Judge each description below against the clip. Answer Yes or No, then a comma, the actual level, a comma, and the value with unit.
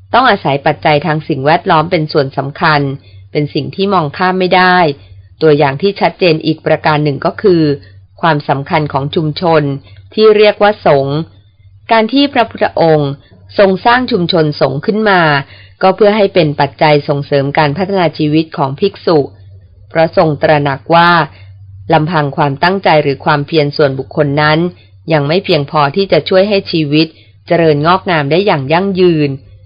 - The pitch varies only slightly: No, average, 4.2 semitones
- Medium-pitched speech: Yes, medium, 155 Hz